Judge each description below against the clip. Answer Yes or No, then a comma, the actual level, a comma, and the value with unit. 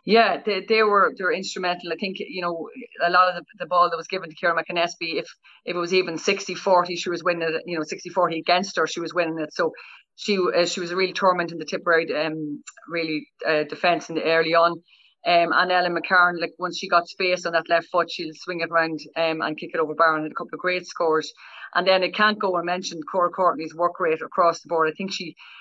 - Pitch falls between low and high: Yes, medium, 175 Hz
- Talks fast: Yes, fast, 260 wpm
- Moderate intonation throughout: No, narrow, 1.9 semitones